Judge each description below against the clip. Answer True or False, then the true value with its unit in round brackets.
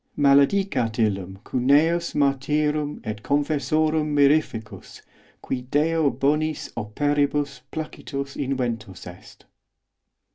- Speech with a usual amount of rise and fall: True (3.5 semitones)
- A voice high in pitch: False (140 Hz)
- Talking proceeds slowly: True (80 wpm)